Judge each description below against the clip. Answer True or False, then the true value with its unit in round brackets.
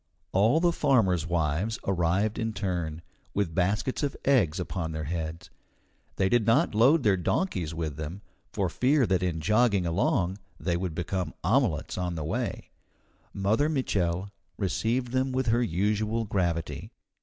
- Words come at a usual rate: True (150 wpm)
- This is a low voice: True (95 Hz)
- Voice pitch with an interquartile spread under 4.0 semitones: False (5.0 semitones)